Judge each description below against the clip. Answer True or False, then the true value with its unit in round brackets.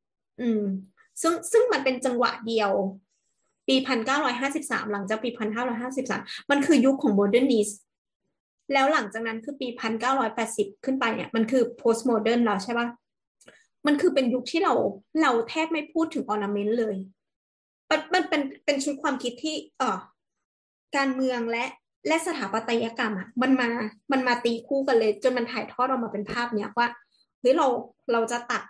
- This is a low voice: False (245 Hz)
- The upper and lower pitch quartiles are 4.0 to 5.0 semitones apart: False (3.6 semitones)